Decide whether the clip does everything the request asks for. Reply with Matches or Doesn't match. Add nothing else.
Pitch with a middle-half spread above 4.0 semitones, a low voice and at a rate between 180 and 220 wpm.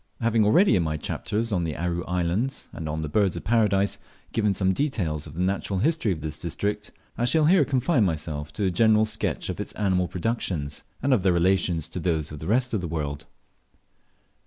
Matches